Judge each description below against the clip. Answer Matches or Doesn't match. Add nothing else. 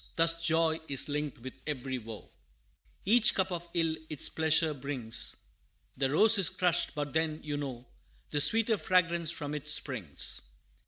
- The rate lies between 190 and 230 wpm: Doesn't match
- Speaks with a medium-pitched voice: Matches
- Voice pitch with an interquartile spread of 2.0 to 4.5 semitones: Matches